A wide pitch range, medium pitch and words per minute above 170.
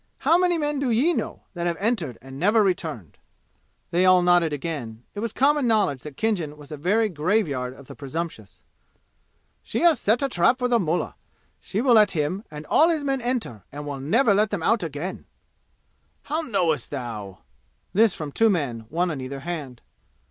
Yes: wide, 7.7 semitones; medium, 175 Hz; average, 190 wpm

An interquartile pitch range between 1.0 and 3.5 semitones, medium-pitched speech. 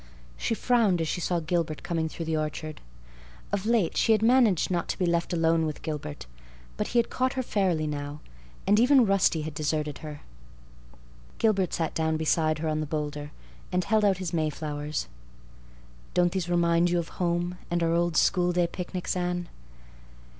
Yes: average, 3.0 semitones; medium, 170 Hz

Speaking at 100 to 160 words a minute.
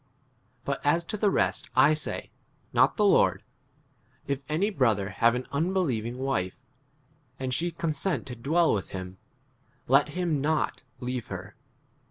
Yes: average, 150 wpm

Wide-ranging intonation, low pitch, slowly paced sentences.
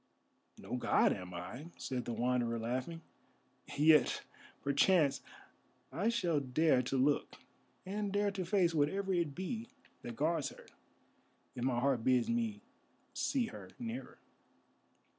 No: wide, 7.5 semitones; medium, 150 Hz; slow, 130 wpm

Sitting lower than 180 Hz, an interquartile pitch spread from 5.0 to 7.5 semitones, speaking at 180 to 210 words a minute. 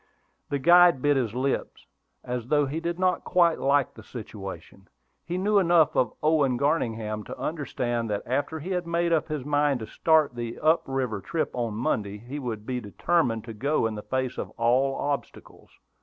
Yes: low, 135 Hz; wide, 5.5 semitones; average, 190 wpm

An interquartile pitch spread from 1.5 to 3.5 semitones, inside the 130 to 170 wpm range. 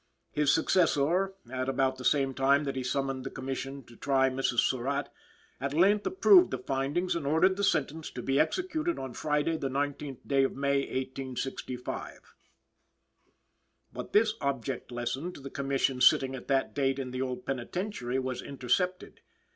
Yes: average, 2.9 semitones; average, 165 wpm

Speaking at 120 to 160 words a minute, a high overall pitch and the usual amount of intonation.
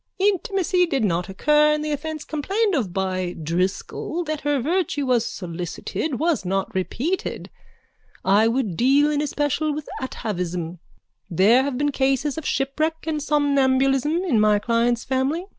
No: average, 145 wpm; very high, 275 Hz; wide, 6.4 semitones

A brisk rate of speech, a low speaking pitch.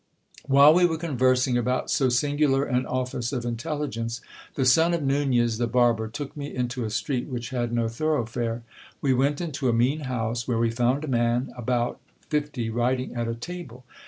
No: average, 185 wpm; low, 125 Hz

